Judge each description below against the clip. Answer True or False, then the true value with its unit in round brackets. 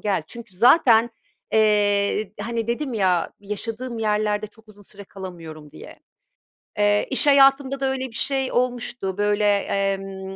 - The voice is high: True (210 Hz)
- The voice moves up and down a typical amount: True (3.4 semitones)